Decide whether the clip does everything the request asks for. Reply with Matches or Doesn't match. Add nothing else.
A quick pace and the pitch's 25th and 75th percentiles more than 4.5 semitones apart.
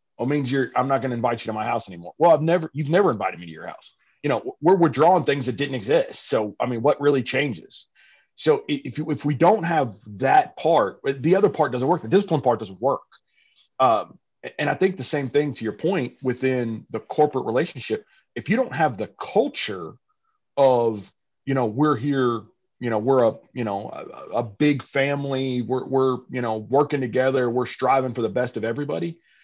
Doesn't match